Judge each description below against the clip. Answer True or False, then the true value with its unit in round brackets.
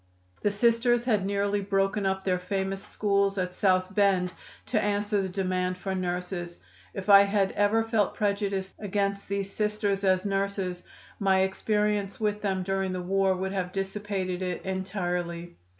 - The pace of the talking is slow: False (155 wpm)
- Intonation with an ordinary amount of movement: False (1.6 semitones)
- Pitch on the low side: False (195 Hz)